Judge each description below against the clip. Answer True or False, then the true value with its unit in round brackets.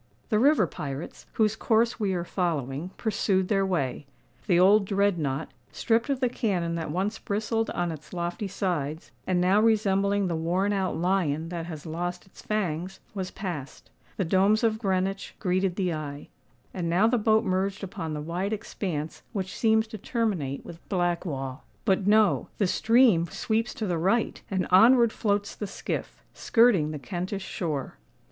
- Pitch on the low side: False (190 Hz)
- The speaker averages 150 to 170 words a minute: True (160 wpm)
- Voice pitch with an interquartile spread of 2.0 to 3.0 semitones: False (4.0 semitones)